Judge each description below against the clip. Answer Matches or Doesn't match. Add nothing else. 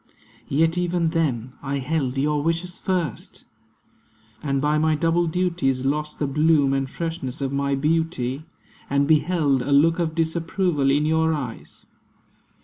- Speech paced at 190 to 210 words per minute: Doesn't match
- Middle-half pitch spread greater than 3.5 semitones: Doesn't match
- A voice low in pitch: Doesn't match